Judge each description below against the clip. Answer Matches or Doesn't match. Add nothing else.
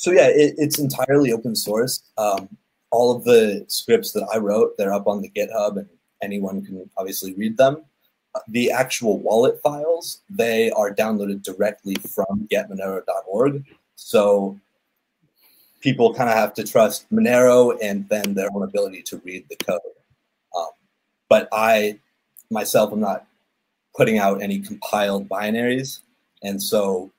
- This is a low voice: Matches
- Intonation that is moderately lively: Doesn't match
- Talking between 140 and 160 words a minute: Matches